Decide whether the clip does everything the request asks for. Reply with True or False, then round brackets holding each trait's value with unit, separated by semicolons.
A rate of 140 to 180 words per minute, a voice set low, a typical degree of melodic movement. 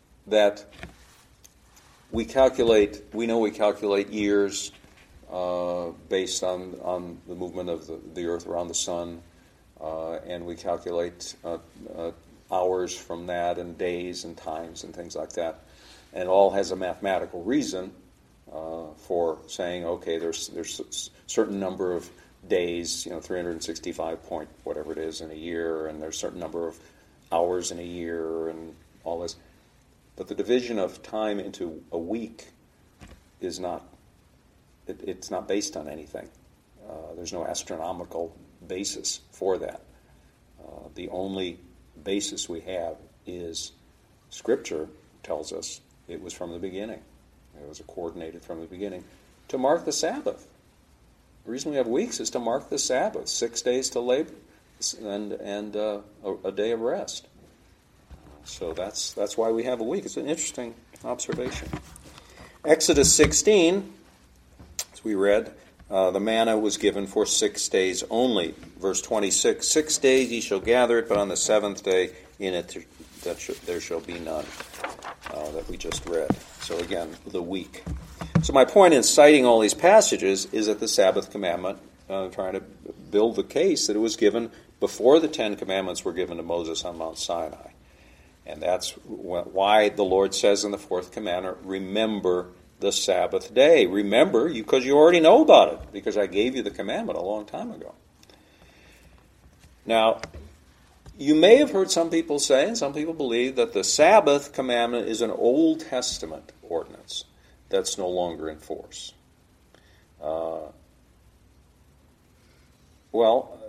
True (160 wpm; 90 Hz; 4.6 semitones)